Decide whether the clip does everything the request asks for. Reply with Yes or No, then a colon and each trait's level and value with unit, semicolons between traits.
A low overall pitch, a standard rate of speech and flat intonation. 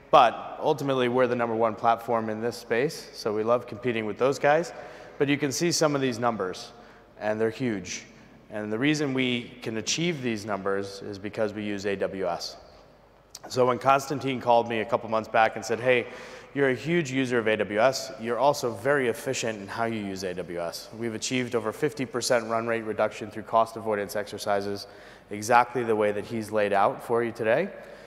No: low, 115 Hz; average, 190 wpm; average, 3.0 semitones